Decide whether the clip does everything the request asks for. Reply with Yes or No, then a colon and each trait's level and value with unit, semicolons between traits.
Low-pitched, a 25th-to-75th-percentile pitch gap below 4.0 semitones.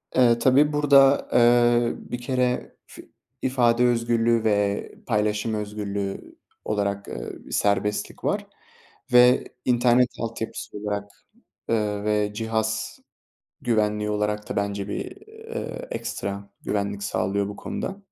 Yes: low, 110 Hz; average, 2.9 semitones